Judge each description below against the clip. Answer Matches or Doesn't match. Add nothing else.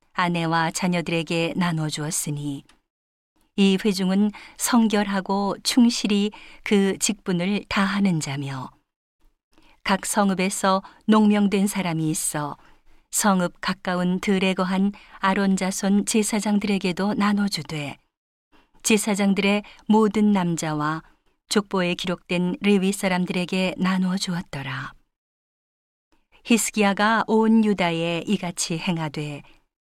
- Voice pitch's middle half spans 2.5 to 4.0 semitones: Matches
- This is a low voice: Doesn't match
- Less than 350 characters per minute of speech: Matches